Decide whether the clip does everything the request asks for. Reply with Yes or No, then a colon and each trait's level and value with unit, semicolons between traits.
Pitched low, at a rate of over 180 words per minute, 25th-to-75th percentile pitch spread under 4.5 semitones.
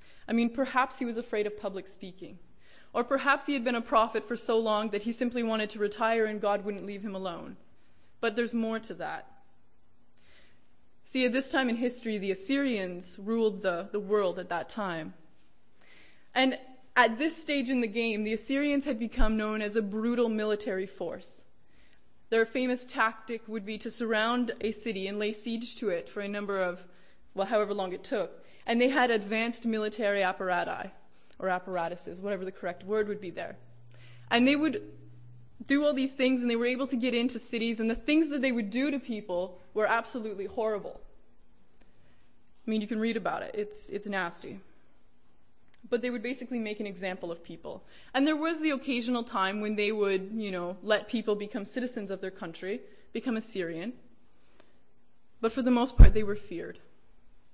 No: high, 220 Hz; average, 190 wpm; average, 3.8 semitones